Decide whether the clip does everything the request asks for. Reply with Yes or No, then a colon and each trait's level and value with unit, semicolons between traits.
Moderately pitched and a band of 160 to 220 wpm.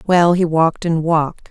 Yes: medium, 165 Hz; average, 200 wpm